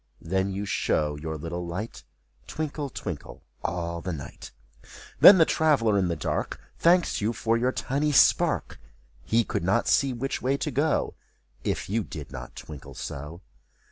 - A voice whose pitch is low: Yes, low, 105 Hz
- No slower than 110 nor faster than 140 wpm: No, average, 160 wpm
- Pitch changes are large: Yes, wide, 8.3 semitones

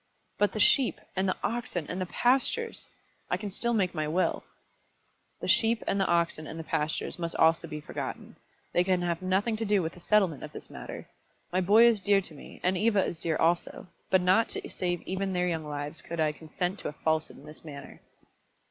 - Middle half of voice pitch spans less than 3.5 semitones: No, average, 3.9 semitones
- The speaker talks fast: Yes, fast, 215 wpm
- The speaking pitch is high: No, medium, 180 Hz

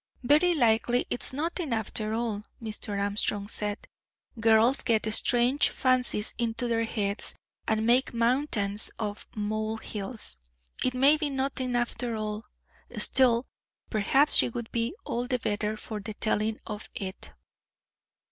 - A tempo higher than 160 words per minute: No, slow, 135 wpm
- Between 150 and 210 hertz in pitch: No, high, 230 Hz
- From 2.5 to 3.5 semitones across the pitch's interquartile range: Yes, average, 2.9 semitones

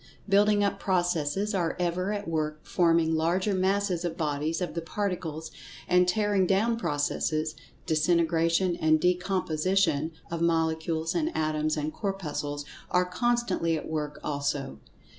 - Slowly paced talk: Yes, slow, 125 wpm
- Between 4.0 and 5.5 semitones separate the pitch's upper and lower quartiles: No, average, 3.3 semitones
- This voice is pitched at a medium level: Yes, medium, 170 Hz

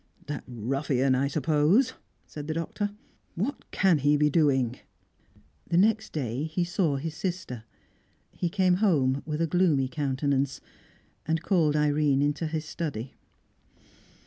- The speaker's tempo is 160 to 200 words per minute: No, slow, 135 wpm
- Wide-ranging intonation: No, average, 3.7 semitones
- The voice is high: No, medium, 150 Hz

